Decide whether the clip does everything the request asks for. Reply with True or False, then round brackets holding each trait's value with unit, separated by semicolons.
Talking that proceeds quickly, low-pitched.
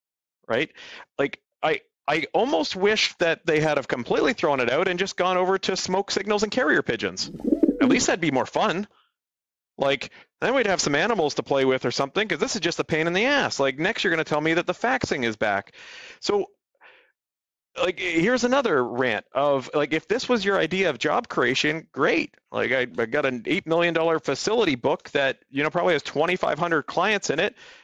False (210 wpm; 185 Hz)